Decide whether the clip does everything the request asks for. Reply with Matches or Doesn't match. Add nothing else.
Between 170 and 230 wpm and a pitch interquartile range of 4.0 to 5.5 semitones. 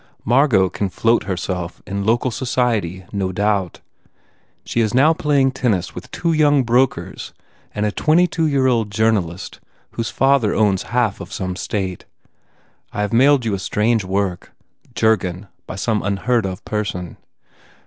Doesn't match